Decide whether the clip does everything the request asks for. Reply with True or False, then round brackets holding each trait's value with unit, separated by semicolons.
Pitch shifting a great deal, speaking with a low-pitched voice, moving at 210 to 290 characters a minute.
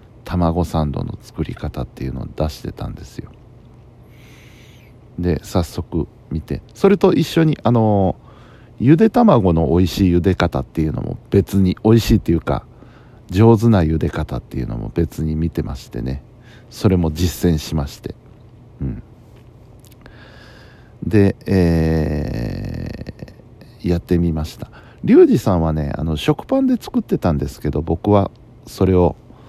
True (6.6 semitones; 105 Hz; 270 characters per minute)